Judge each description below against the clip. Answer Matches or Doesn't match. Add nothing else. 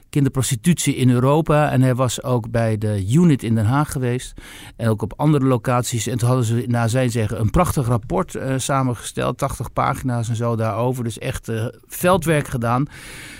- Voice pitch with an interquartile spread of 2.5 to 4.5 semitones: Matches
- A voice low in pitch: Matches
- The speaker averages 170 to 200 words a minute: Matches